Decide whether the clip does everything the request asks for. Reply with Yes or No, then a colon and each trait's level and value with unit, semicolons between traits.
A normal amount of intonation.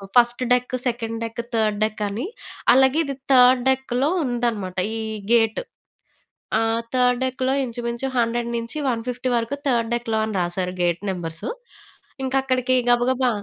No: narrow, 2.2 semitones